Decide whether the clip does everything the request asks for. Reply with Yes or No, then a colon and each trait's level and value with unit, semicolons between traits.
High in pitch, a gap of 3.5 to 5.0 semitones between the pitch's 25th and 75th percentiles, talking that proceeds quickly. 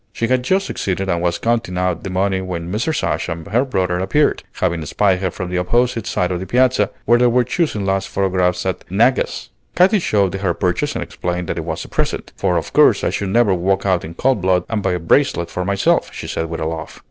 No: very low, 95 Hz; average, 4.5 semitones; fast, 240 wpm